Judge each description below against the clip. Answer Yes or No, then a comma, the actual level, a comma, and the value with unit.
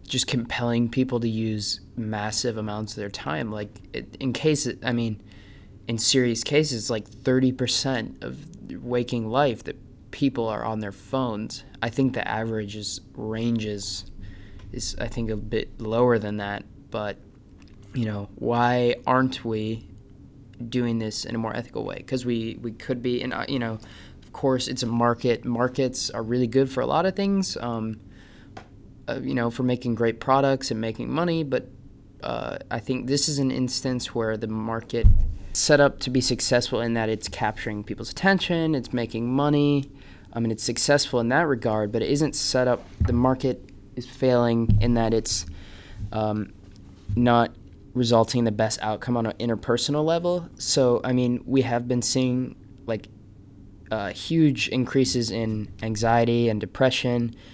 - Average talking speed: Yes, average, 170 wpm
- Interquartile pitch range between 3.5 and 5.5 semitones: No, average, 3.1 semitones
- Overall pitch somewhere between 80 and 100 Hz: No, low, 115 Hz